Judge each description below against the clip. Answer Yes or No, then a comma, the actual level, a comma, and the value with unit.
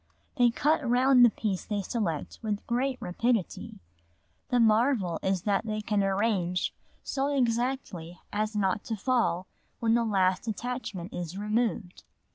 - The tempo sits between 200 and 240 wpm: No, average, 140 wpm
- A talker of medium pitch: No, high, 215 Hz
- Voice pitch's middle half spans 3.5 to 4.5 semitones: Yes, average, 4.2 semitones